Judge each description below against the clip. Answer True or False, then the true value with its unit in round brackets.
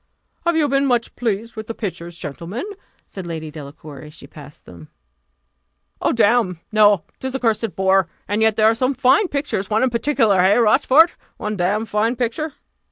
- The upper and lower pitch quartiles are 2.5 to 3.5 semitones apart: False (5.2 semitones)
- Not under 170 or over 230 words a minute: True (180 wpm)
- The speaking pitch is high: True (215 Hz)